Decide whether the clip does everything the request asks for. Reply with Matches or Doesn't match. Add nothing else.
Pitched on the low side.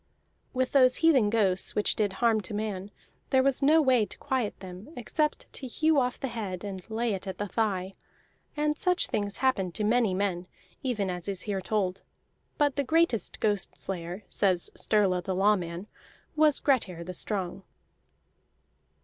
Doesn't match